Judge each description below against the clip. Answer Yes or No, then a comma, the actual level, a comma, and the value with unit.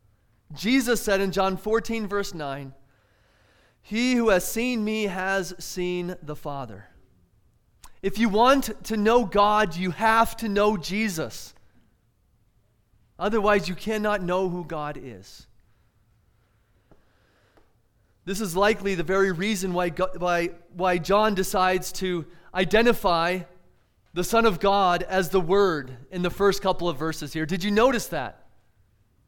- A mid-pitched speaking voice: Yes, medium, 180 Hz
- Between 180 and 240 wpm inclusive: No, slow, 135 wpm